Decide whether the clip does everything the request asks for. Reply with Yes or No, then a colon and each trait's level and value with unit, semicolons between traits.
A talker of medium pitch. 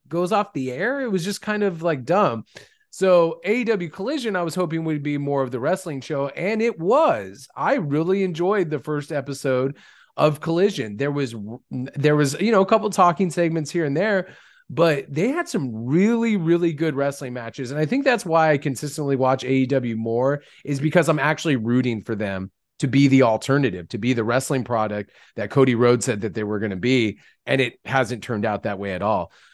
Yes: medium, 145 Hz